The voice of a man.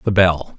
Yes: male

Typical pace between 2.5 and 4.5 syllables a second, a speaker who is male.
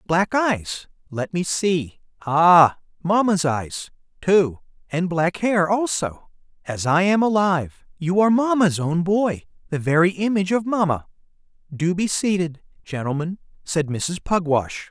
Yes: 4.2 syllables/s; male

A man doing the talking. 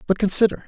Yes: male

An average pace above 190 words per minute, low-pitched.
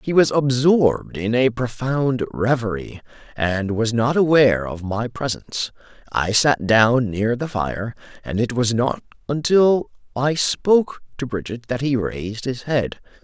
No: average, 155 wpm; low, 125 Hz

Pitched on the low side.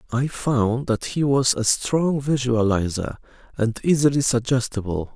Yes: low, 125 Hz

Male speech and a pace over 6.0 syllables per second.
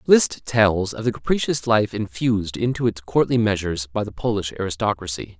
No: male; 5.5 syllables/s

